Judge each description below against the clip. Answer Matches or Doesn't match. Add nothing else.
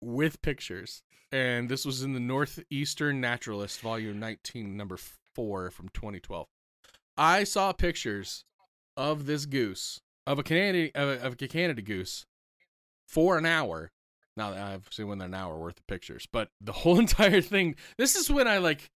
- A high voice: Doesn't match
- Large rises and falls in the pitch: Matches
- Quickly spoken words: Doesn't match